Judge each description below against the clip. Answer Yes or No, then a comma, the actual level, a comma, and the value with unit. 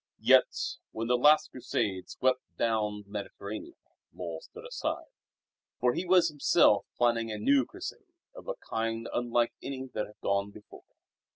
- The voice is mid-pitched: No, low, 115 Hz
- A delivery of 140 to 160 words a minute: Yes, average, 155 wpm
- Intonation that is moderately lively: Yes, average, 3.9 semitones